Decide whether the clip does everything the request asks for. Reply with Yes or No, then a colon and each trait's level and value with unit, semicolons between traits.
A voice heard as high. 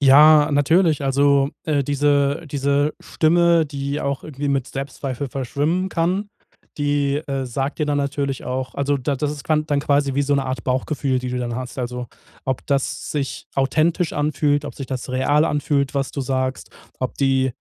No: medium, 140 Hz